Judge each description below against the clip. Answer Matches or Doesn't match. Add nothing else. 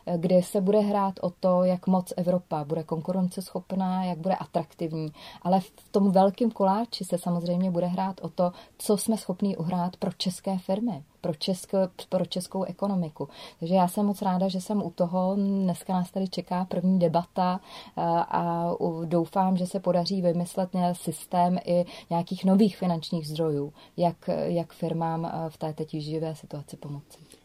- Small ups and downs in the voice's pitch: Matches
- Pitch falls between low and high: Matches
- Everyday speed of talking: Matches